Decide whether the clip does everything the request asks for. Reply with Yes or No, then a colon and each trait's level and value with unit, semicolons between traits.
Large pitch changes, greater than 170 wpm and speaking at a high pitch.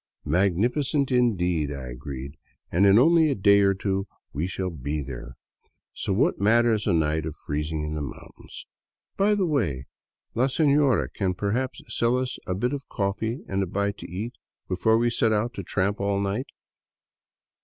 No: wide, 6.8 semitones; average, 180 wpm; low, 100 Hz